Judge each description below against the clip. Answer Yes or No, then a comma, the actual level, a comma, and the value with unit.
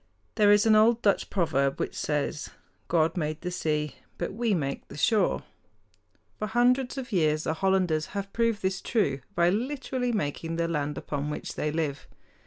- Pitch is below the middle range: No, medium, 180 Hz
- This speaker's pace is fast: No, average, 175 wpm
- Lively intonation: Yes, wide, 6.1 semitones